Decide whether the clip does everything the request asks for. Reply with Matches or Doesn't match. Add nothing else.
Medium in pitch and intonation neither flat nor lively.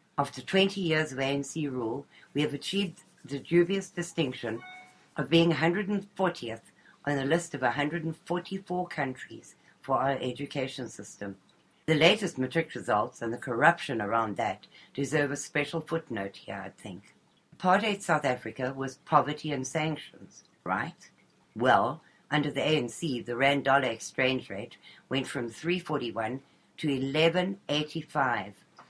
Matches